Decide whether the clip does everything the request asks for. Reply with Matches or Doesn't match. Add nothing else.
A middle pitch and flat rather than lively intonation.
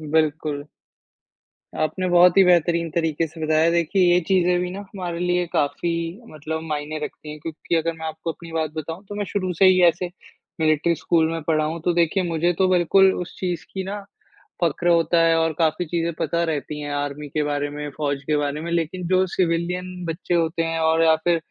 Matches